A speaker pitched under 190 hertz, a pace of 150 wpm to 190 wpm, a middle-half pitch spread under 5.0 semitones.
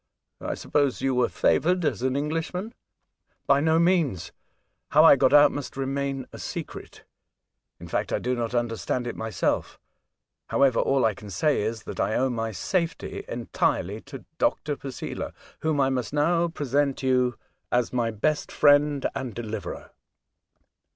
Yes: low, 135 Hz; average, 160 wpm; average, 3.6 semitones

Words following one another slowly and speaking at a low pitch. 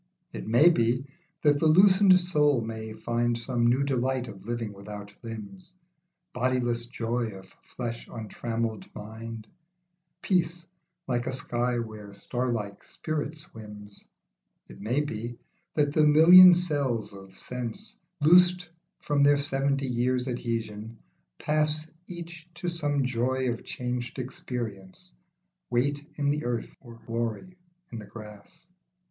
Yes: slow, 130 wpm; low, 125 Hz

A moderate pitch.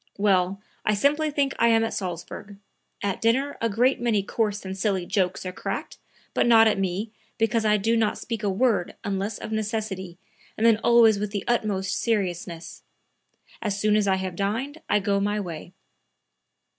No: high, 210 Hz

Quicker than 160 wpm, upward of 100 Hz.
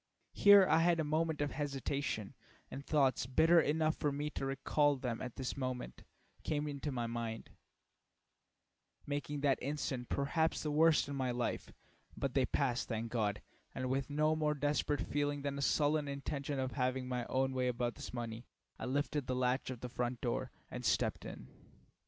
Yes: average, 180 wpm; medium, 140 Hz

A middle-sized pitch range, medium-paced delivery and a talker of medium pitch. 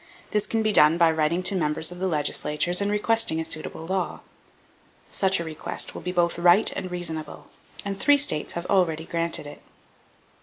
Yes: average, 3.1 semitones; average, 185 wpm; medium, 175 Hz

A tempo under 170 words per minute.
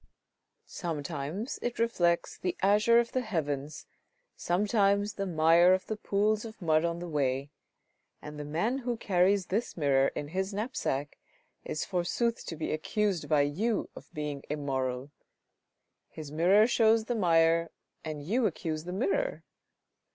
Yes: average, 145 wpm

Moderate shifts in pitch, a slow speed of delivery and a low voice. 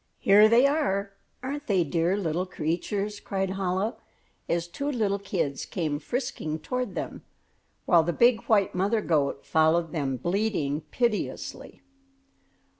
No: average, 4.8 semitones; slow, 130 wpm; high, 190 Hz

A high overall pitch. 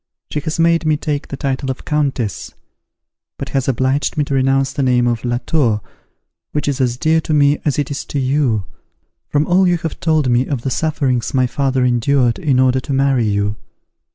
No: low, 135 Hz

